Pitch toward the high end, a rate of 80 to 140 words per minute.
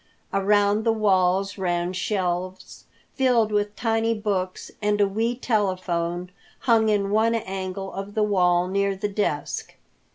Yes: high, 200 Hz; slow, 135 wpm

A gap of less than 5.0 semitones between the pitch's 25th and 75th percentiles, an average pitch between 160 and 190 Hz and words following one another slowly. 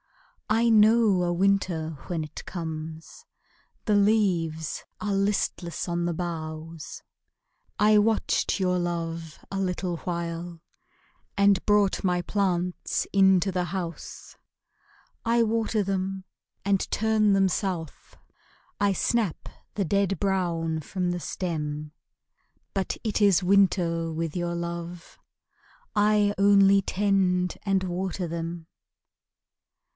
Yes: average, 2.9 semitones; medium, 185 Hz; slow, 110 wpm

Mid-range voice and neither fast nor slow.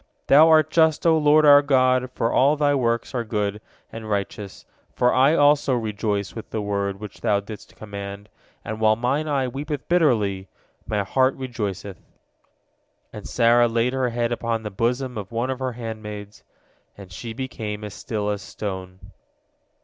No: low, 115 Hz; average, 170 wpm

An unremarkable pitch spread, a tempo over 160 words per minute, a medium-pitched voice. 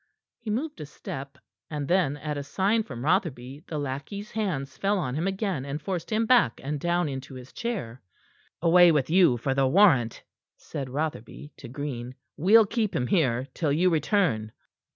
No: wide, 6.2 semitones; average, 175 wpm; medium, 150 Hz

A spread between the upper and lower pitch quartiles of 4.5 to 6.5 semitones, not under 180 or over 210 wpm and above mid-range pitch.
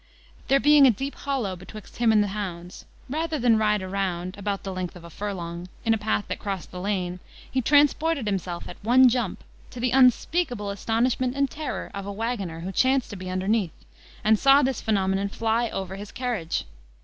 Yes: average, 4.9 semitones; average, 195 wpm; high, 210 Hz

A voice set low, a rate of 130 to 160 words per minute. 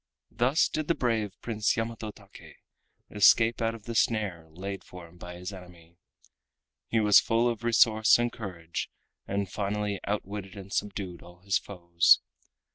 Yes: low, 100 Hz; average, 155 wpm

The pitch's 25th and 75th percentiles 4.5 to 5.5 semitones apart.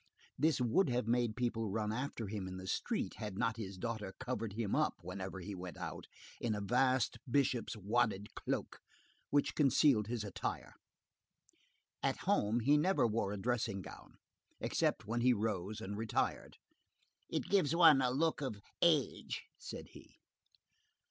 No: average, 3.9 semitones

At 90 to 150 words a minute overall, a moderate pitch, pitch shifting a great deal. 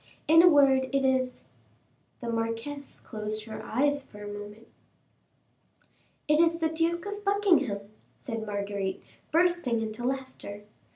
No: slow, 135 wpm; very high, 260 Hz; wide, 6.7 semitones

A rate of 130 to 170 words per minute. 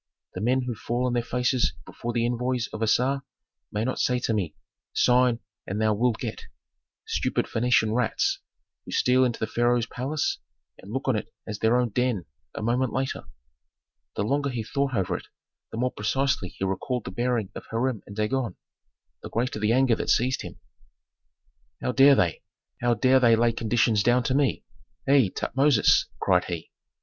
No: average, 180 wpm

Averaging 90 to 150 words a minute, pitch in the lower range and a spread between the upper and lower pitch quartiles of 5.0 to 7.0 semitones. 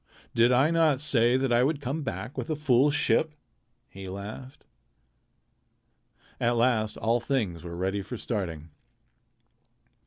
Yes: slow, 135 wpm; low, 120 Hz; wide, 5.4 semitones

